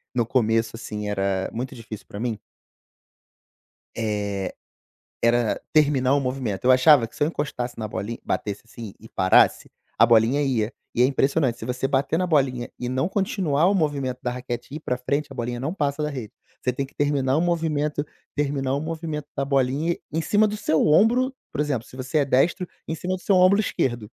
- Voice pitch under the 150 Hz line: Yes, low, 135 Hz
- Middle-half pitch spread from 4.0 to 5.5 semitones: Yes, average, 4.3 semitones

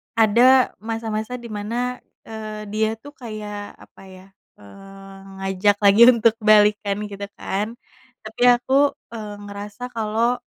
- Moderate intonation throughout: No, narrow, 2.3 semitones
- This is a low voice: No, high, 215 Hz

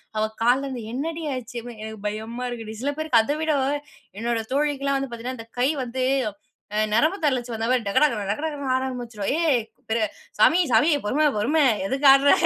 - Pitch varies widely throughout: No, average, 3.8 semitones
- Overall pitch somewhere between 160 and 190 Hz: No, very high, 250 Hz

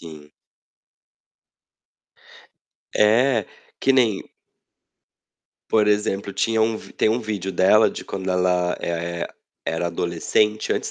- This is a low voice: Yes, low, 100 Hz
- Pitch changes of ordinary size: Yes, average, 3.9 semitones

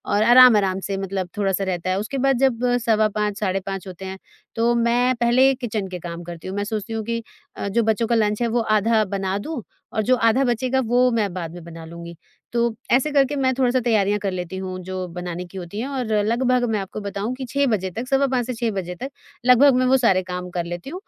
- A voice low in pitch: No, high, 215 Hz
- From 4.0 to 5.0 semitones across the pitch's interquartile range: Yes, average, 4.7 semitones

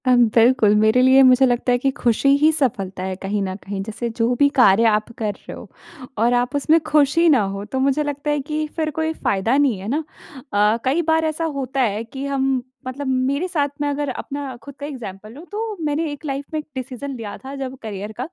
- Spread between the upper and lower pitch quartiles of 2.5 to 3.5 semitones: No, average, 4.4 semitones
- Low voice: No, very high, 260 Hz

